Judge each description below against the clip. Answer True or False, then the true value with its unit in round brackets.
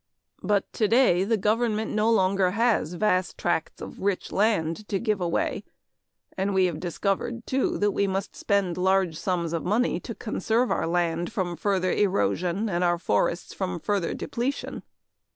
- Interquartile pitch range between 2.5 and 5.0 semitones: True (3.4 semitones)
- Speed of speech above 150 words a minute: True (160 wpm)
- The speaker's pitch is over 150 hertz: True (190 Hz)